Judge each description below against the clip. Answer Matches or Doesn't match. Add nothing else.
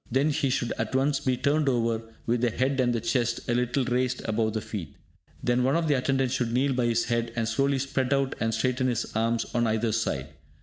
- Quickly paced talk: Matches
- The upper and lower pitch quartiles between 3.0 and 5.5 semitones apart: Doesn't match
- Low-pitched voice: Matches